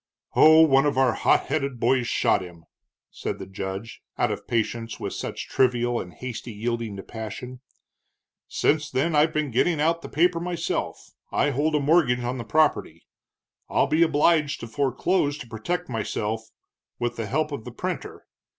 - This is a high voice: No, low, 130 Hz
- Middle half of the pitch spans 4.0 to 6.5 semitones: Yes, average, 5.1 semitones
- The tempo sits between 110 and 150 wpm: No, average, 170 wpm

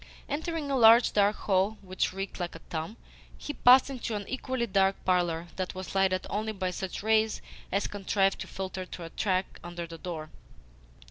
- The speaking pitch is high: Yes, high, 195 Hz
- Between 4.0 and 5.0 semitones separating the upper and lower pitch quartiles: No, average, 3.2 semitones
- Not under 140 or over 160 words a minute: No, average, 185 wpm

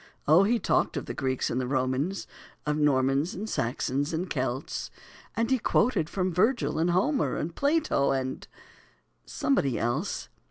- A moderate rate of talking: Yes, average, 155 wpm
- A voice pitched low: No, medium, 155 Hz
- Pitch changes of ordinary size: No, wide, 7.1 semitones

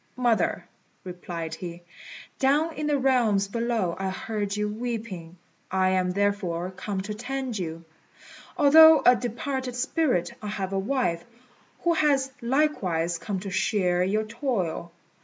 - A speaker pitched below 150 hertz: No, high, 210 Hz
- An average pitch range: No, wide, 5.8 semitones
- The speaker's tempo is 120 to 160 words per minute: Yes, average, 140 wpm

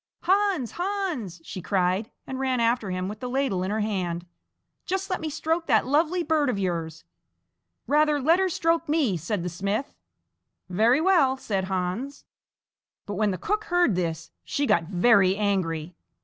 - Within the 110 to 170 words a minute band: Yes, average, 165 wpm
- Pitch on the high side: Yes, high, 230 Hz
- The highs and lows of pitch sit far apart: Yes, wide, 9.0 semitones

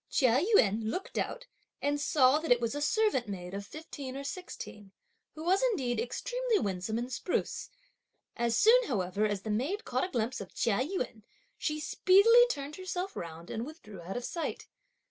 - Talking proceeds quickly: No, average, 180 wpm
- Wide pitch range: Yes, wide, 9.0 semitones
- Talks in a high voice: Yes, very high, 260 Hz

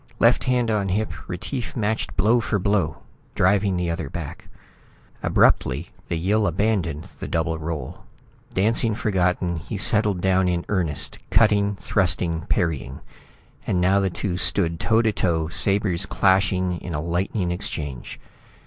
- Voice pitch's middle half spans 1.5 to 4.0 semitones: Yes, average, 3.4 semitones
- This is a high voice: No, very low, 95 Hz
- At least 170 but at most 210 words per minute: No, average, 140 wpm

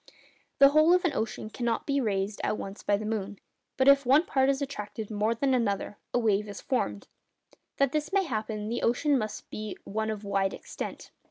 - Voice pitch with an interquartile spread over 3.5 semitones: Yes, average, 4.9 semitones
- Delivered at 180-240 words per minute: Yes, average, 200 wpm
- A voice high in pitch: Yes, high, 225 Hz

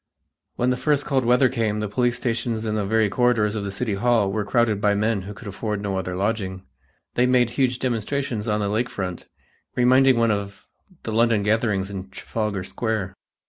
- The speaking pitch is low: Yes, low, 110 Hz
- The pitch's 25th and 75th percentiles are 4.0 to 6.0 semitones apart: No, average, 3.2 semitones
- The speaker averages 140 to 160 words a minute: No, average, 195 wpm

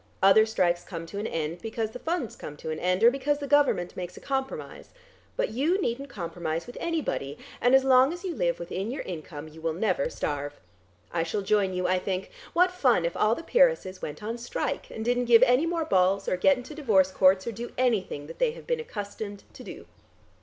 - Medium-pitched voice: No, high, 215 Hz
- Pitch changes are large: Yes, wide, 6.9 semitones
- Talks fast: Yes, fast, 220 wpm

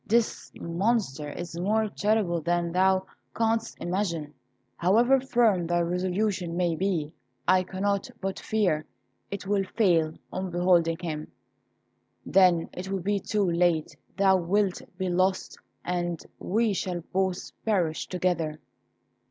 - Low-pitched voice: No, medium, 185 Hz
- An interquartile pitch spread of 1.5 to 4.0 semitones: Yes, average, 2.7 semitones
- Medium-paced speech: No, slow, 125 wpm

